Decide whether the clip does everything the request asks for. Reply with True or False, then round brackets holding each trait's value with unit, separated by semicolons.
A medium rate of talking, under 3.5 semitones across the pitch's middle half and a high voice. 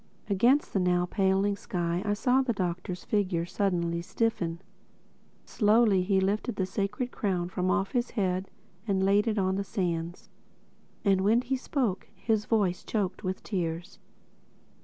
True (155 wpm; 2.8 semitones; 195 Hz)